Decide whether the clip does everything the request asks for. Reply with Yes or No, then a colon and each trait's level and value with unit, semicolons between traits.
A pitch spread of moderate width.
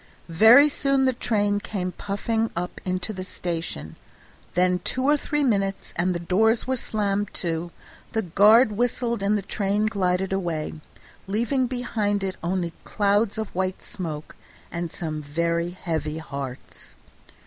Yes: average, 4.3 semitones